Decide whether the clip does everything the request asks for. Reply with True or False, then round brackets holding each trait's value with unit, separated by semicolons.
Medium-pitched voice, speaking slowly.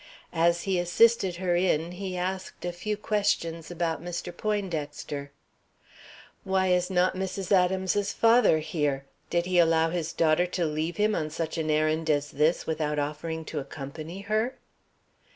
False (175 Hz; 150 wpm)